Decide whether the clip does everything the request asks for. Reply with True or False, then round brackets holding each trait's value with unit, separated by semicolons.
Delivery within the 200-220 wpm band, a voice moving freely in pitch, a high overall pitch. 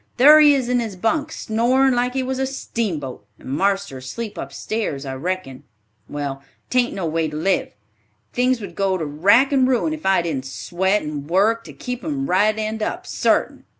False (190 wpm; 7.7 semitones; 210 Hz)